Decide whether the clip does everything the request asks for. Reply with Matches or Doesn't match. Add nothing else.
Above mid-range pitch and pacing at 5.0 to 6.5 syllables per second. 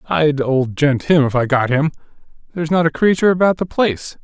Doesn't match